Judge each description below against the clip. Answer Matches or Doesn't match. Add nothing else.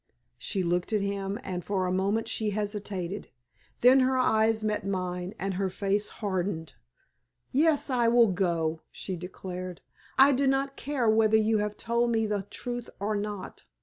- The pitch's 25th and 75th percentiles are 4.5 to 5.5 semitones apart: Doesn't match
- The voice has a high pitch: Matches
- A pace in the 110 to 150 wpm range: Doesn't match